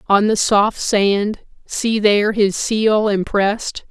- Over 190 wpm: No, average, 140 wpm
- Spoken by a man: No, female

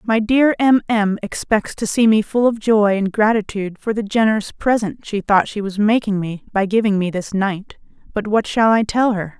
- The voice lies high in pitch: Yes, high, 210 Hz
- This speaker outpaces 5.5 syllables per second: No, 5.0 syllables/s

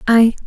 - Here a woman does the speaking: No, male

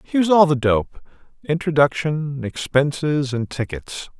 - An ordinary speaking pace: No, slow, 100 wpm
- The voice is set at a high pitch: No, medium, 145 Hz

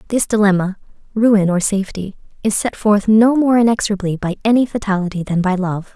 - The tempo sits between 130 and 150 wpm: No, average, 170 wpm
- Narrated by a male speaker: No, female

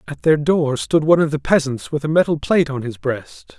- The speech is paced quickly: Yes, fast, 250 wpm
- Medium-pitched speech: Yes, medium, 145 Hz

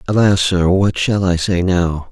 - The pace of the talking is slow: No, average, 200 wpm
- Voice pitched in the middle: No, very low, 90 Hz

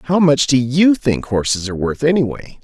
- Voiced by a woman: No, male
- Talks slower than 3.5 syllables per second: No, 5.4 syllables/s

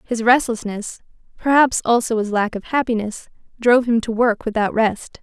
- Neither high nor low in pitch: No, high, 230 Hz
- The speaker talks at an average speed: Yes, average, 160 wpm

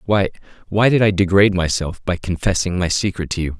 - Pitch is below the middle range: Yes, very low, 95 Hz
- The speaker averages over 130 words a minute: Yes, average, 200 wpm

